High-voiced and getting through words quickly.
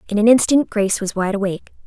Yes: high, 210 Hz; fast, 225 wpm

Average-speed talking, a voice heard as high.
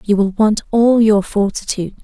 Yes: average, 175 wpm; high, 210 Hz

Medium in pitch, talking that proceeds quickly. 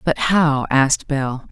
No: medium, 145 Hz; average, 160 wpm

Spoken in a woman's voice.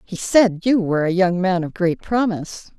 Yes: female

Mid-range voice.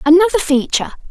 No: very high, 340 Hz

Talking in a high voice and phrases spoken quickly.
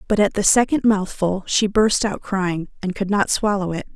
Yes: high, 200 Hz; fast, 210 wpm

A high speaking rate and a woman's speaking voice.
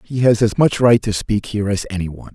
No: fast, 280 wpm; male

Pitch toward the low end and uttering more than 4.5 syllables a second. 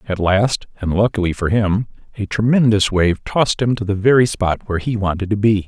Yes: low, 105 Hz; 5.6 syllables/s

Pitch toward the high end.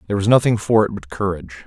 No: low, 100 Hz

